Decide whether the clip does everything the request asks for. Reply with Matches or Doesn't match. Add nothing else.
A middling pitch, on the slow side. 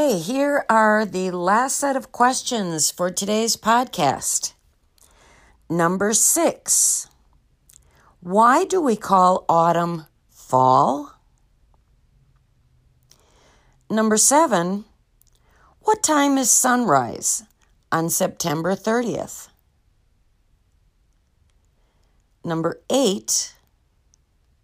Matches